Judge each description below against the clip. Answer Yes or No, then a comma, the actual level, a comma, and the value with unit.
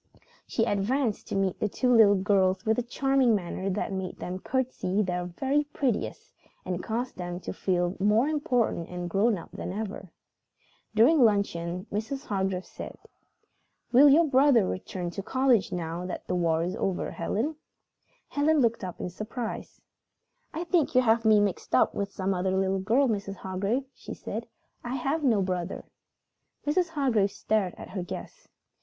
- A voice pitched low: No, high, 205 Hz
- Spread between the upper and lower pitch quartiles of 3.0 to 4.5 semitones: No, wide, 5.4 semitones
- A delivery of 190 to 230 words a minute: No, average, 165 wpm